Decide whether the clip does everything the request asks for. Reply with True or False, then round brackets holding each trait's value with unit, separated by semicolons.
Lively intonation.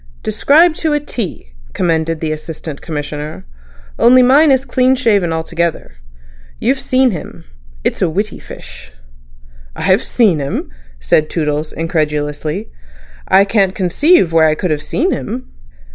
True (8.3 semitones)